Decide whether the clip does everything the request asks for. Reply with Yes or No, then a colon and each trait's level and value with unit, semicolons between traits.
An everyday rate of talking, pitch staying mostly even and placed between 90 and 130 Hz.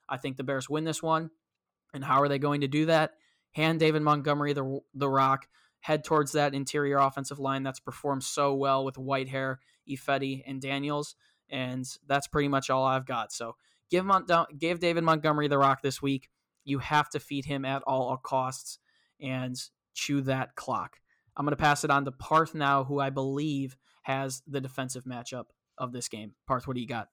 No: average, 195 wpm; narrow, 1.8 semitones; medium, 140 Hz